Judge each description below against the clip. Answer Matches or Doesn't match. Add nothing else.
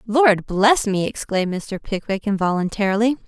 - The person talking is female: Matches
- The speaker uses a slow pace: Matches